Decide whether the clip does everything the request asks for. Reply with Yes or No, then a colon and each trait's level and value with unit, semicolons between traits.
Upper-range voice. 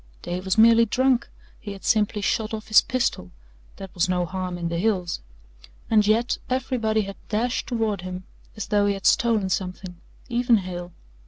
Yes: high, 205 Hz